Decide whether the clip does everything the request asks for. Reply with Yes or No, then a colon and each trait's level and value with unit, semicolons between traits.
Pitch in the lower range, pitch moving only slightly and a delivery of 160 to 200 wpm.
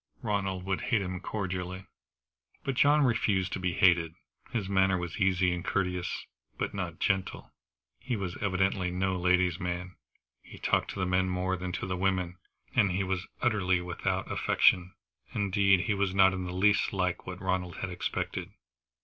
Yes: very low, 95 Hz; narrow, 1.3 semitones; average, 170 wpm